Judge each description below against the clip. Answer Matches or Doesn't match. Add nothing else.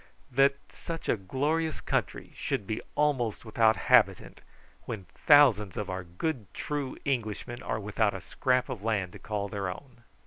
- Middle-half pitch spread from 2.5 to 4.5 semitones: Doesn't match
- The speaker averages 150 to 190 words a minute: Matches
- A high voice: Doesn't match